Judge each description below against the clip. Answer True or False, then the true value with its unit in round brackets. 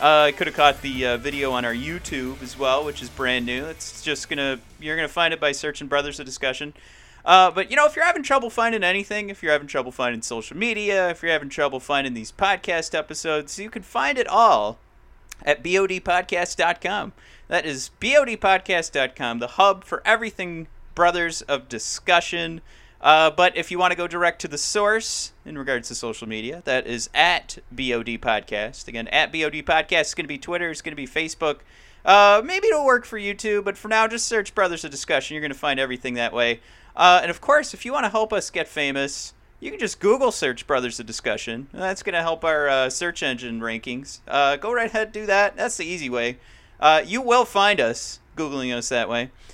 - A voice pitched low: False (155 Hz)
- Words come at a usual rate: False (215 wpm)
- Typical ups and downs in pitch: False (6.9 semitones)